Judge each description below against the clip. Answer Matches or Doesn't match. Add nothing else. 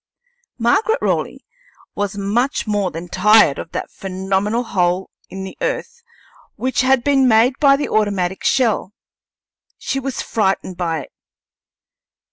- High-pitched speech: Matches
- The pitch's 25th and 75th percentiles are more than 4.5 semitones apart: Matches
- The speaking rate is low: Matches